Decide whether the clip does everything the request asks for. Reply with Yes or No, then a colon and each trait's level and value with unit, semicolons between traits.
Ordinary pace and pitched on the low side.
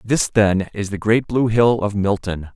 No: fast, 210 wpm; low, 105 Hz